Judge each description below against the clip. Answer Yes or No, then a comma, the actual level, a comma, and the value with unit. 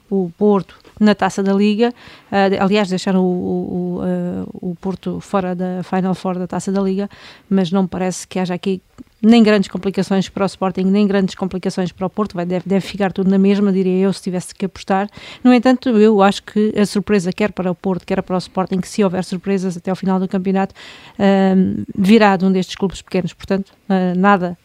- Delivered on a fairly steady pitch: Yes, narrow, 1.4 semitones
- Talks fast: Yes, fast, 215 wpm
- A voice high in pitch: Yes, high, 195 Hz